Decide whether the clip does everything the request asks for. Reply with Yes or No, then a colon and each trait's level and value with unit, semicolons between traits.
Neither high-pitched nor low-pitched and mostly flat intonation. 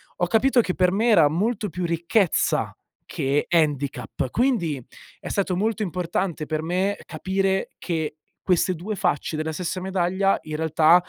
No: medium, 180 Hz; average, 3.4 semitones